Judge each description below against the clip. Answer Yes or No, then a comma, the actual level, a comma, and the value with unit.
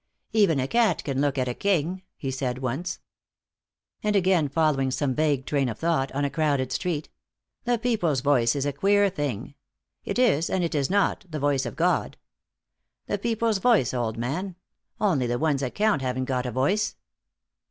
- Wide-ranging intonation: Yes, wide, 6.4 semitones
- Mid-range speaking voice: Yes, medium, 145 Hz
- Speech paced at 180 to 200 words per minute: Yes, average, 185 wpm